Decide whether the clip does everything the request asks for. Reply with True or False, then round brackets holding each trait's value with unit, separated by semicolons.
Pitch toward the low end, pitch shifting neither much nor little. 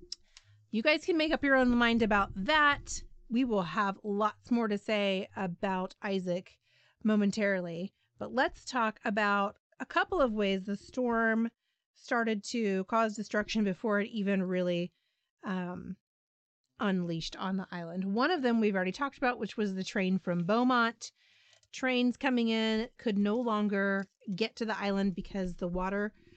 False (210 Hz; 3.4 semitones)